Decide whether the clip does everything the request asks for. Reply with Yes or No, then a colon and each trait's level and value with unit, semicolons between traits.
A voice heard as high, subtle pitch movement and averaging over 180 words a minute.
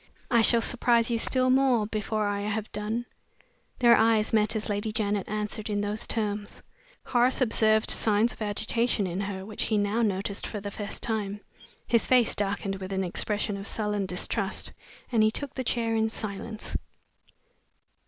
No: high, 215 Hz; narrow, 2.0 semitones; average, 170 wpm